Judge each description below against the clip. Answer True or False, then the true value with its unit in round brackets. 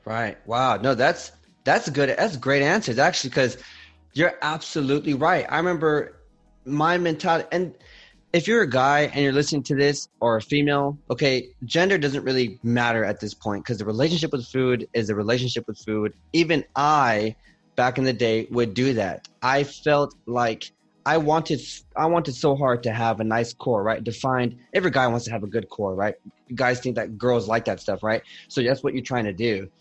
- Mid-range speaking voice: False (130 Hz)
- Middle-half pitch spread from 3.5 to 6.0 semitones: True (4.0 semitones)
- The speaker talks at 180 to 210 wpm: True (200 wpm)